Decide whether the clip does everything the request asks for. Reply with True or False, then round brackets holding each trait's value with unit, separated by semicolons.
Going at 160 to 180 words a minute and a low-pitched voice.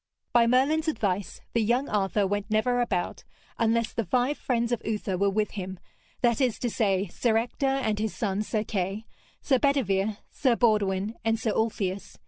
False (175 wpm; 220 Hz)